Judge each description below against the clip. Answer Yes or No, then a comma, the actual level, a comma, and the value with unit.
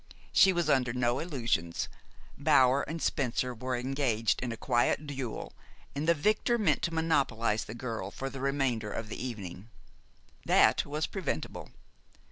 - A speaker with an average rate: Yes, average, 150 wpm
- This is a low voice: Yes, low, 130 Hz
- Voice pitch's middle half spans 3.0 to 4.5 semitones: Yes, average, 4.1 semitones